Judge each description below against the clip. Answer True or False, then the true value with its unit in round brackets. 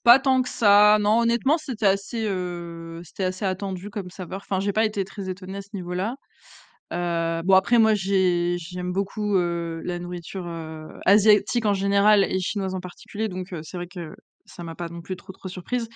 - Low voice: False (190 Hz)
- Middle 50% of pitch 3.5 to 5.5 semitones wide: False (2.9 semitones)